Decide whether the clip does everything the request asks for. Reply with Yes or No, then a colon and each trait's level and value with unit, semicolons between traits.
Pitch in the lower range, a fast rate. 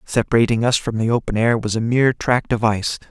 Yes: low, 115 Hz; fast, 230 wpm